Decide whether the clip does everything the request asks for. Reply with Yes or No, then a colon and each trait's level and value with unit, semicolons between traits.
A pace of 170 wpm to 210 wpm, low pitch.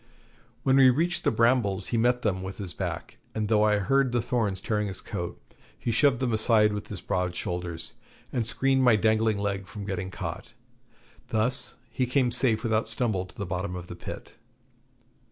Yes: average, 190 wpm; low, 110 Hz